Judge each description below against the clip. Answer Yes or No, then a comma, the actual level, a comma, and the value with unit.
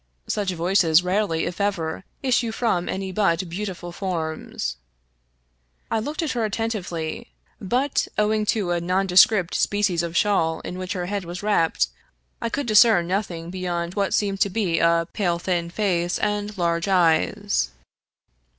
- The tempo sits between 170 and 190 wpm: No, average, 150 wpm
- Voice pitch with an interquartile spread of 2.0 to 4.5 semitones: Yes, average, 3.4 semitones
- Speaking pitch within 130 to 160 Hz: No, medium, 185 Hz